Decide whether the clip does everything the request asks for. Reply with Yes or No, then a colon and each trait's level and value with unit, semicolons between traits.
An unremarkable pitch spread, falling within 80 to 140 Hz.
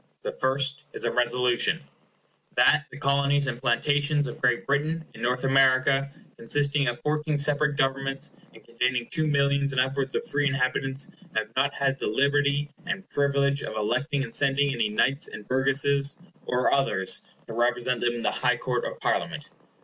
No: narrow, 2.1 semitones; low, 135 Hz